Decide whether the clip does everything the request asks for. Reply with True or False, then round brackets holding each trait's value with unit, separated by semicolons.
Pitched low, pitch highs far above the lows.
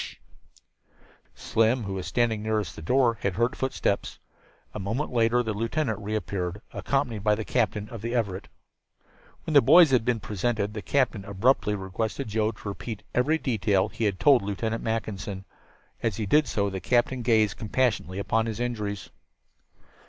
False (110 Hz; 3.1 semitones)